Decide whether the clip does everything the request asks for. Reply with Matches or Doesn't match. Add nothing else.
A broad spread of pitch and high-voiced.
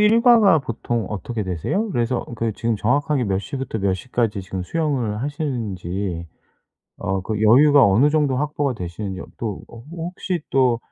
Doesn't match